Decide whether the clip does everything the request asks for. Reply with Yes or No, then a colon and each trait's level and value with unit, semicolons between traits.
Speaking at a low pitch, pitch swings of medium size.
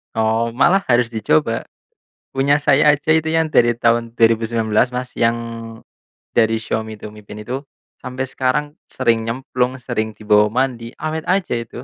Yes: low, 120 Hz; average, 3.1 semitones